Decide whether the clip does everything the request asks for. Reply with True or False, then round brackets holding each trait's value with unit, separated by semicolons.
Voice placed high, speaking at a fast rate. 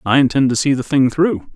False (135 Hz; 270 wpm)